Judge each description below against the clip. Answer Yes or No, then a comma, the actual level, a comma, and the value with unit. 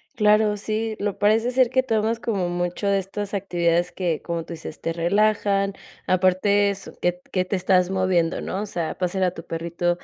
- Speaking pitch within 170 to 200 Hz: Yes, high, 190 Hz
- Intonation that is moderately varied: Yes, average, 3.0 semitones